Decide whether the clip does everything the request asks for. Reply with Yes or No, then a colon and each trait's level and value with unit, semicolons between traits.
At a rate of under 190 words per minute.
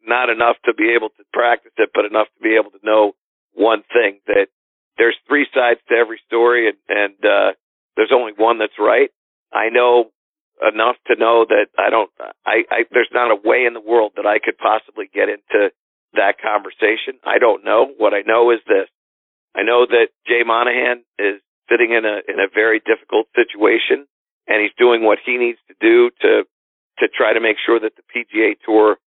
No: average, 200 wpm